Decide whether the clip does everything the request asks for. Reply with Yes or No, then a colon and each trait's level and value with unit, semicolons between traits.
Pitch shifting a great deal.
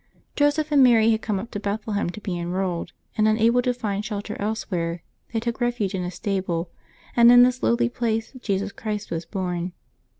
No: average, 3.9 semitones